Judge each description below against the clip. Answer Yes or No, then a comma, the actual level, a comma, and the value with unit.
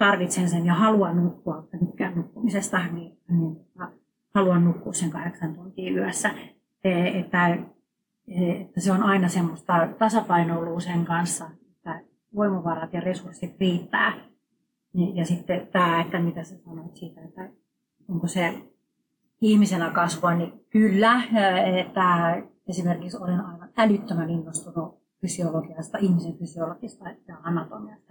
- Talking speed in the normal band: Yes, average, 125 wpm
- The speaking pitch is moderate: Yes, medium, 175 Hz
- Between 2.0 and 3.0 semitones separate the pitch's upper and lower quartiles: Yes, narrow, 2.5 semitones